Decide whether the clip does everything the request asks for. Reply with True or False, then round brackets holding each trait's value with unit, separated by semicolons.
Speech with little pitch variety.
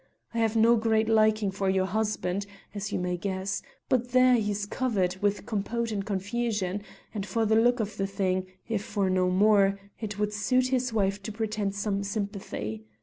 True (2.3 semitones)